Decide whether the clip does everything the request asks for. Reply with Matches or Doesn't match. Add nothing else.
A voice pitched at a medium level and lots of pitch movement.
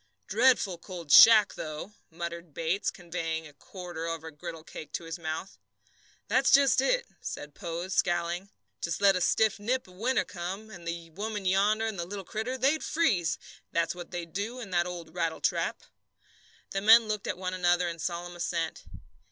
Doesn't match